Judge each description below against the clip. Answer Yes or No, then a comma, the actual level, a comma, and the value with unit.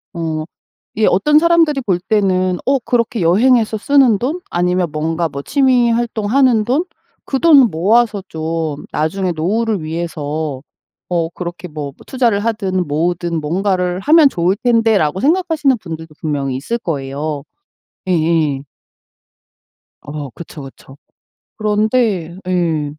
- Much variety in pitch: Yes, wide, 6.5 semitones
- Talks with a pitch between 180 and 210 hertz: Yes, medium, 185 Hz